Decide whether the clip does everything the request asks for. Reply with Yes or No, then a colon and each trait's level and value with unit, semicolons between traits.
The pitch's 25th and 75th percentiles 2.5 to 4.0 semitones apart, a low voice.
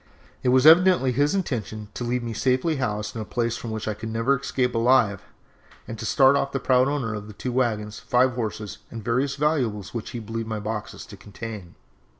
Yes: average, 3.3 semitones; low, 120 Hz